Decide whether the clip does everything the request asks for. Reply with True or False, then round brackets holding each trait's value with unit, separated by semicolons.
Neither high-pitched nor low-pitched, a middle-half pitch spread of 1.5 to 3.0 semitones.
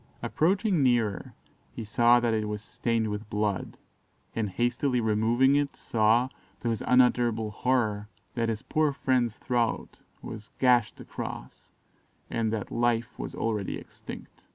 False (115 Hz; 2.5 semitones)